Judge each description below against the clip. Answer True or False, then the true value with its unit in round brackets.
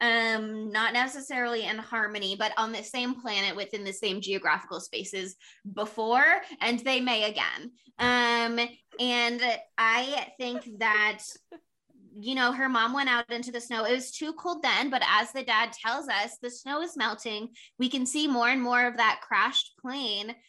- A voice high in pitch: True (235 Hz)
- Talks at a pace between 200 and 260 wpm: False (175 wpm)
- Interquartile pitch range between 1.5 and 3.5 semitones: True (2.6 semitones)